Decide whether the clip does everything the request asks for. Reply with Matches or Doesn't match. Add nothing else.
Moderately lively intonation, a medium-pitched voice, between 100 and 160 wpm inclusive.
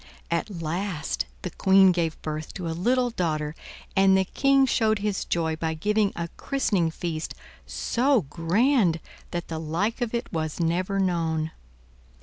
Matches